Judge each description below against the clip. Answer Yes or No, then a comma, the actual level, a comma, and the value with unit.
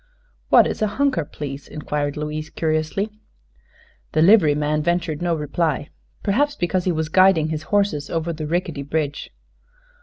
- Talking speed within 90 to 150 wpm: Yes, average, 145 wpm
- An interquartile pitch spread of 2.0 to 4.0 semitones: Yes, average, 3.5 semitones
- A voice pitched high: No, medium, 160 Hz